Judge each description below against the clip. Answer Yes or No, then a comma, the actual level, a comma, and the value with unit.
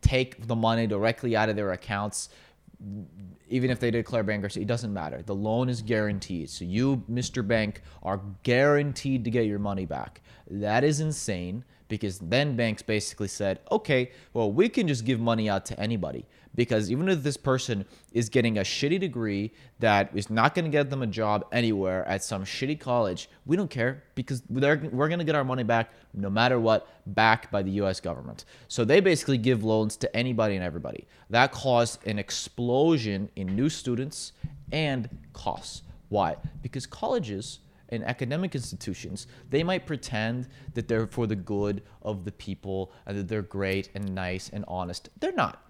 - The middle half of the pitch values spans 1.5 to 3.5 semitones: No, average, 4.3 semitones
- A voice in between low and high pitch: No, low, 115 Hz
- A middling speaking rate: Yes, average, 180 wpm